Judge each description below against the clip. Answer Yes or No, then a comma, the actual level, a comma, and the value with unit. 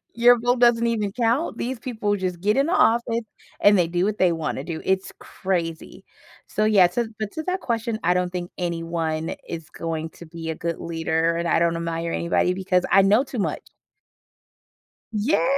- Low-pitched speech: No, high, 190 Hz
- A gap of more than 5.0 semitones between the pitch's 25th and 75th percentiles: Yes, wide, 5.5 semitones